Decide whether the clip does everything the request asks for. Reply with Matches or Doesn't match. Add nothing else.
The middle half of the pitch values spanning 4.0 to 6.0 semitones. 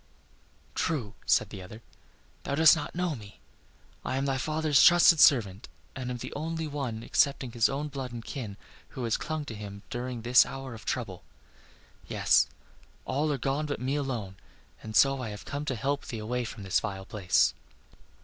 Matches